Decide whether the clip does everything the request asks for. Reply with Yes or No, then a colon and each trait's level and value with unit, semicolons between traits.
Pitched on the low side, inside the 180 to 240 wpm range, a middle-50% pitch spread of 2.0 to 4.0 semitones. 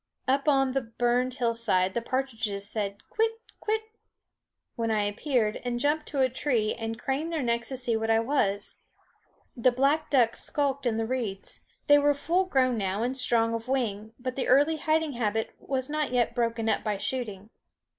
No: high, 245 Hz; average, 185 wpm; average, 3.5 semitones